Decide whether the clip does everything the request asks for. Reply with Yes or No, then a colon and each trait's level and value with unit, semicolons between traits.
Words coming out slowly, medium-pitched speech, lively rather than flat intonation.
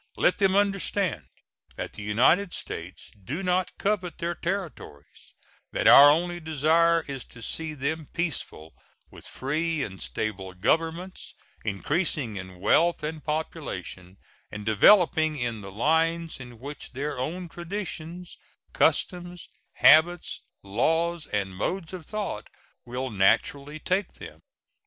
Yes: slow, 125 wpm; medium, 155 Hz; wide, 6.9 semitones